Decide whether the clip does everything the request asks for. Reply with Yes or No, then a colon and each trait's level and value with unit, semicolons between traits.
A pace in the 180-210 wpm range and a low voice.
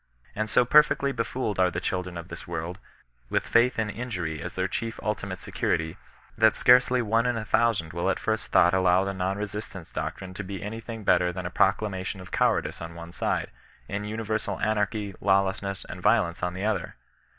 Yes: average, 190 wpm; low, 100 Hz